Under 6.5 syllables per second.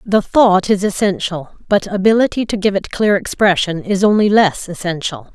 Yes: 4.9 syllables/s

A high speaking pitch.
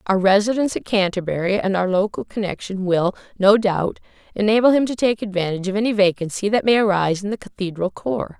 Yes: high, 200 Hz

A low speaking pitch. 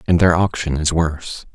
Yes: very low, 80 Hz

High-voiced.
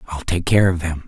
No: very low, 85 Hz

